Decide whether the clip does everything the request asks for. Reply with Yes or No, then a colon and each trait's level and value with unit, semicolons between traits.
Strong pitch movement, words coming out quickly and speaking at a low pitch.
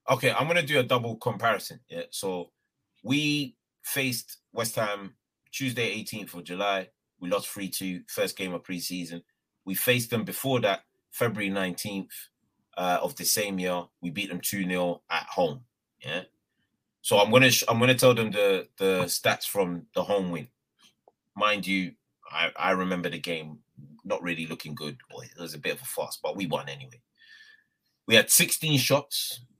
No: wide, 6.1 semitones; average, 175 wpm; low, 100 Hz